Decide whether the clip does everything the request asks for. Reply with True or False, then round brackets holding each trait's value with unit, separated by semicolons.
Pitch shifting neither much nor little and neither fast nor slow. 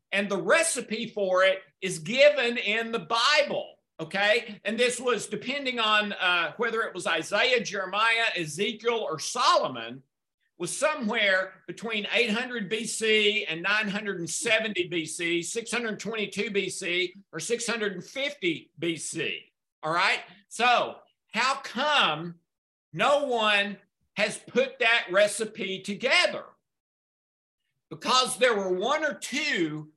False (4.1 semitones; 110 wpm)